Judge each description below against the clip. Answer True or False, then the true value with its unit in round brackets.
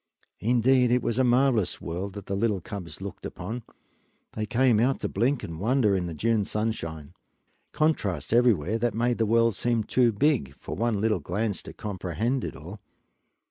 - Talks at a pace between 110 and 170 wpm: False (180 wpm)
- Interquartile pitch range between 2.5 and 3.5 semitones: False (3.9 semitones)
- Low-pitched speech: True (110 Hz)